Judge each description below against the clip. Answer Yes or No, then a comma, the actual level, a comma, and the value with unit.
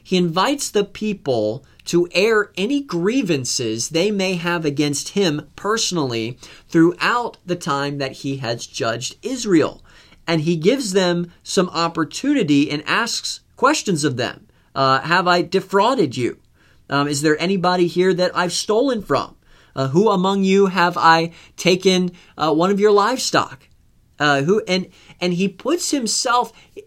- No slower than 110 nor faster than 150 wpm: Yes, average, 145 wpm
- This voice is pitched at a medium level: Yes, medium, 175 Hz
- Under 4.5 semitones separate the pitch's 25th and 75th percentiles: No, average, 5.2 semitones